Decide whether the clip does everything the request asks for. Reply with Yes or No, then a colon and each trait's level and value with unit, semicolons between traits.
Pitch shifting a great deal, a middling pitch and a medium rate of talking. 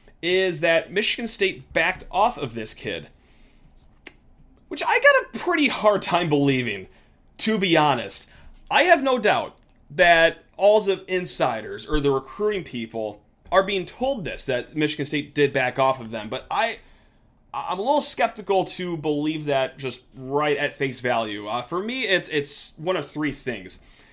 Yes: wide, 6.6 semitones; medium, 150 Hz; average, 165 wpm